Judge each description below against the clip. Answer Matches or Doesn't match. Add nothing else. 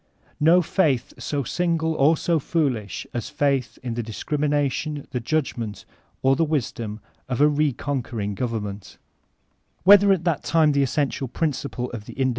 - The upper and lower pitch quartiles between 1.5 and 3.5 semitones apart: Doesn't match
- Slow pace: Doesn't match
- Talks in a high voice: Doesn't match